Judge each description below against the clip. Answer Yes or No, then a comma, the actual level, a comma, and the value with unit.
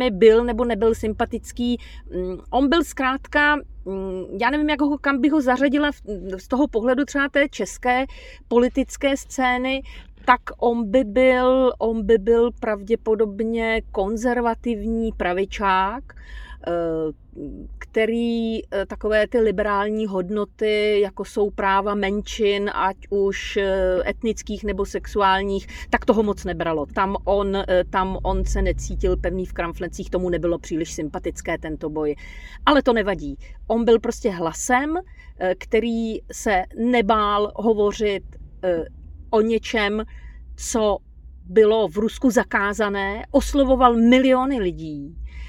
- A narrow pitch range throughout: No, average, 4.1 semitones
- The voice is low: No, high, 215 Hz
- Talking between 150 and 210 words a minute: No, slow, 115 wpm